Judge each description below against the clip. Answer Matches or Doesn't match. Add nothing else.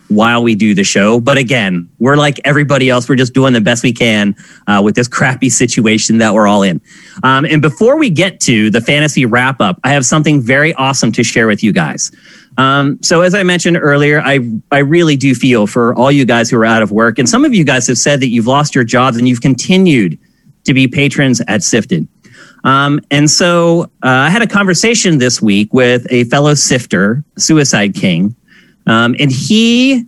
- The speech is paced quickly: Matches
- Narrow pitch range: Doesn't match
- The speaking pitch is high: Doesn't match